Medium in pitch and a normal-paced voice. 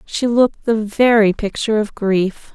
No: high, 215 Hz; average, 165 wpm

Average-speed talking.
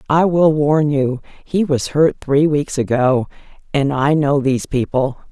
Yes: average, 160 wpm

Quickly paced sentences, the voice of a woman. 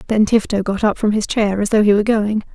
Yes: fast, 285 wpm; female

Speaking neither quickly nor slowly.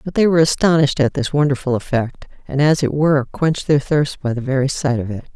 No: fast, 235 wpm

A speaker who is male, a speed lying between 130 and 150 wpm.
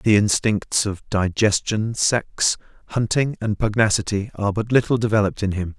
Yes: male; average, 145 wpm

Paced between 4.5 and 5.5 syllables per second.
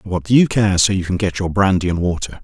No: 6.4 syllables/s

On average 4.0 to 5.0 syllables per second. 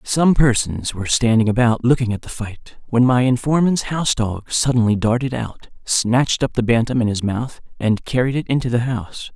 No: 5.2 syllables/s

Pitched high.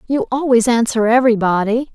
Yes: high, 240 Hz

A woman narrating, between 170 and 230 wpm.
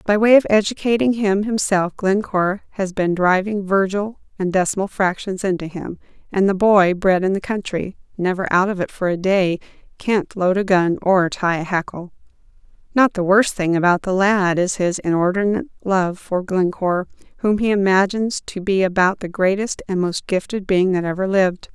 Yes: female; average, 175 wpm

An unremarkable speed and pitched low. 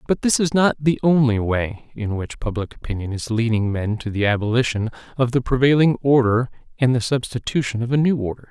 Yes: average, 195 wpm; low, 120 Hz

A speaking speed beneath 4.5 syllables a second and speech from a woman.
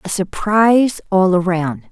Yes: 4.2 syllables/s; female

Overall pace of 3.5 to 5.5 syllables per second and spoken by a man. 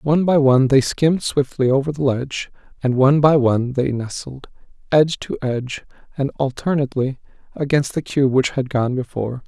No: 5.7 syllables/s; male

